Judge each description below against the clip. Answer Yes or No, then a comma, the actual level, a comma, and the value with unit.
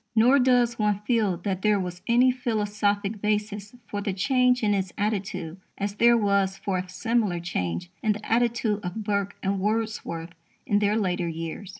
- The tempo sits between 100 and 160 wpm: No, average, 175 wpm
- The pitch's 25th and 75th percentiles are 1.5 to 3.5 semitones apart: Yes, average, 2.7 semitones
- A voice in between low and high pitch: No, high, 205 Hz